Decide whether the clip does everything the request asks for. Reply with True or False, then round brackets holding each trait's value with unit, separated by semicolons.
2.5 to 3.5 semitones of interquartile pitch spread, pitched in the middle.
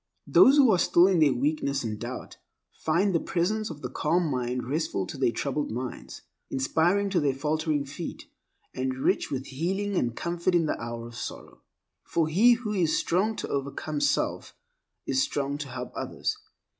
False (5.0 semitones; 150 Hz)